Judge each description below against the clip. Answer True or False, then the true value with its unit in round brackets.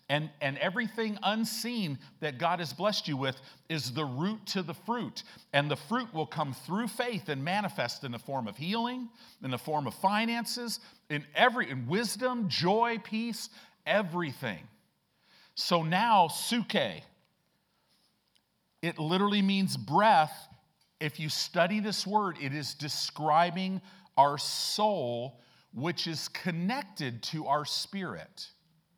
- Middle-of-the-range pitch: True (180 Hz)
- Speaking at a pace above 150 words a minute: False (135 wpm)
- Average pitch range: False (6.2 semitones)